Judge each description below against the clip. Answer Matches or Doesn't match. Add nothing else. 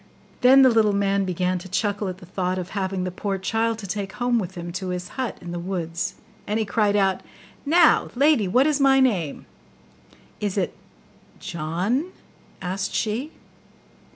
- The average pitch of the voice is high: Matches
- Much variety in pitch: Doesn't match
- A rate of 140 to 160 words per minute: Doesn't match